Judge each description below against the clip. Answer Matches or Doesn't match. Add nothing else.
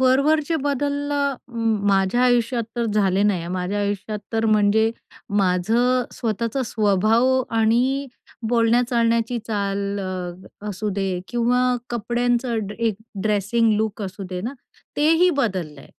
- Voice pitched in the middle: Doesn't match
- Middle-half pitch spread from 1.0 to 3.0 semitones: Doesn't match